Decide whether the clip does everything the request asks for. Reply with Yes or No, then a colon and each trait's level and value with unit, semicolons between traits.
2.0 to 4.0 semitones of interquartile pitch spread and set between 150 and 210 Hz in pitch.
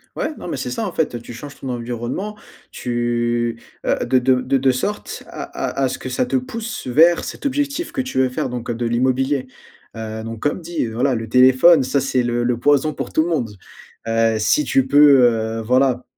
No: average, 3.6 semitones; low, 130 Hz